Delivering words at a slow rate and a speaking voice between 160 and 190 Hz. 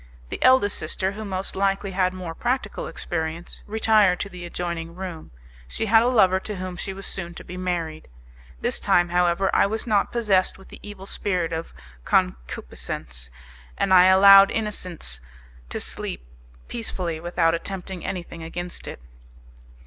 No: average, 155 wpm; medium, 185 Hz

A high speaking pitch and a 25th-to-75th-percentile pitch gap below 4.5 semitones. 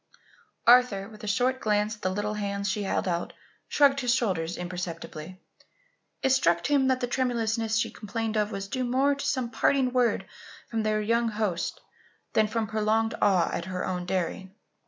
Yes: high, 215 Hz; average, 4.1 semitones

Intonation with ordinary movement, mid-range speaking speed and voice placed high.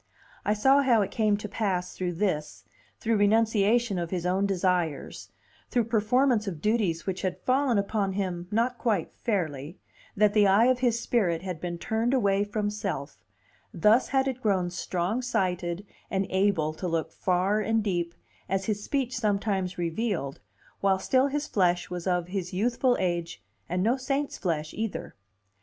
Yes: average, 4.0 semitones; average, 165 wpm; high, 200 Hz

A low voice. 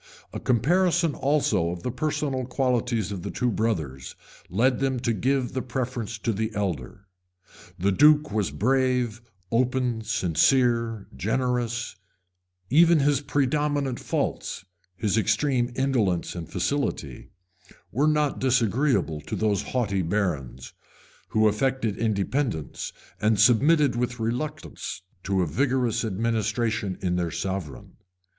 Yes: low, 115 Hz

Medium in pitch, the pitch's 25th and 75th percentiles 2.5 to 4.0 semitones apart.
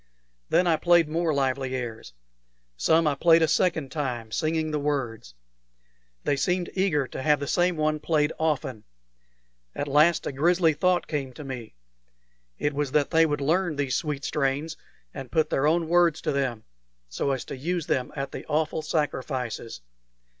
Yes: medium, 150 Hz; average, 3.2 semitones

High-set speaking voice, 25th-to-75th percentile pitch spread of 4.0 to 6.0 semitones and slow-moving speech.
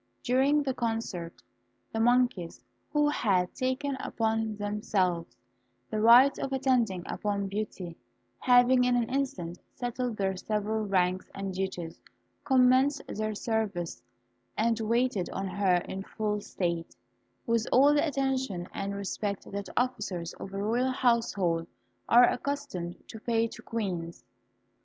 Yes: high, 220 Hz; average, 4.6 semitones; slow, 130 wpm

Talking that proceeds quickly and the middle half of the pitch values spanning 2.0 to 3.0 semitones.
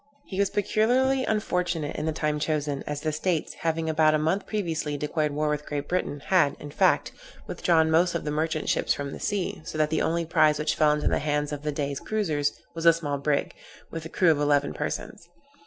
Yes: fast, 220 wpm; narrow, 2.4 semitones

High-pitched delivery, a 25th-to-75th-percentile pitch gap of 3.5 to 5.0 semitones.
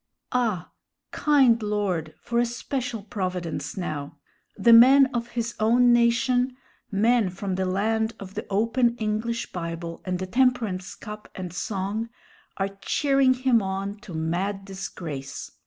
Yes: high, 215 Hz; average, 4.2 semitones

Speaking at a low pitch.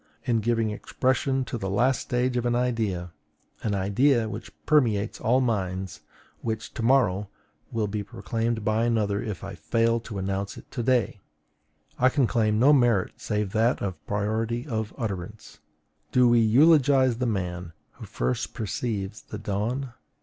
Yes: low, 110 Hz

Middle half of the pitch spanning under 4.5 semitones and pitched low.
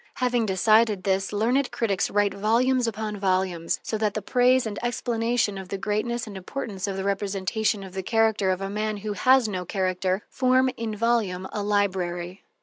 No: average, 3.1 semitones; high, 210 Hz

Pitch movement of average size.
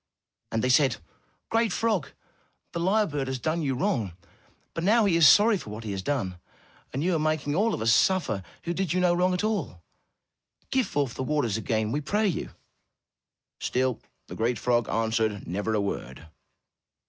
No: wide, 8.4 semitones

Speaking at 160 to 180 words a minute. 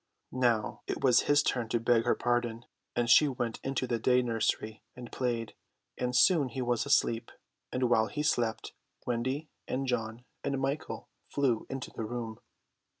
Yes: average, 165 wpm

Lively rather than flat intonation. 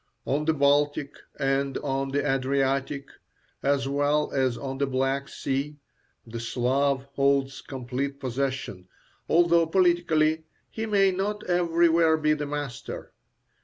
No: average, 2.8 semitones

